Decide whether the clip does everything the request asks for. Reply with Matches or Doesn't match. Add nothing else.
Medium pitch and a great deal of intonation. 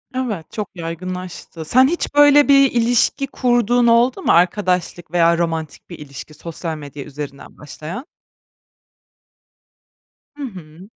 Matches